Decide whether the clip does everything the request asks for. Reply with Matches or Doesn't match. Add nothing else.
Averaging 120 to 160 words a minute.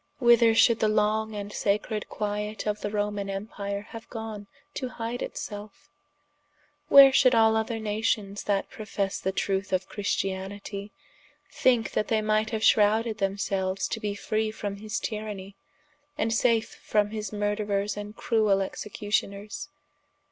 Matches